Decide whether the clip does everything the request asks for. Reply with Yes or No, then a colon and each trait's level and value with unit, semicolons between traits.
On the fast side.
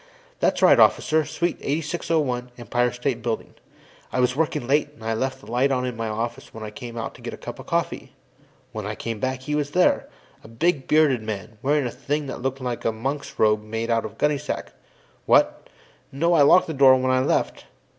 Yes: fast, 215 wpm